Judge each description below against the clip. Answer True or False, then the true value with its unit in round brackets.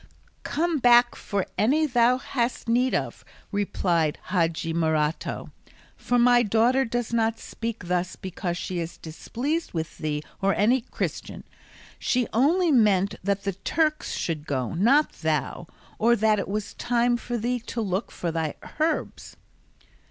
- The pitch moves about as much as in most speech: False (5.7 semitones)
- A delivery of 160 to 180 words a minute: False (145 wpm)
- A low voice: False (220 Hz)